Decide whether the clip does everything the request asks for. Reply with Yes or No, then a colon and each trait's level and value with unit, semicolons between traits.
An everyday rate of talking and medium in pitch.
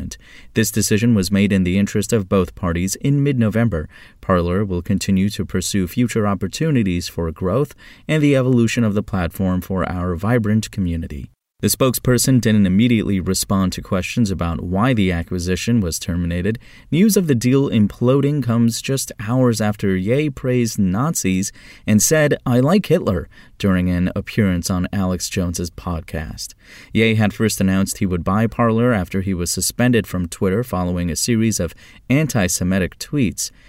No: average, 160 wpm; low, 100 Hz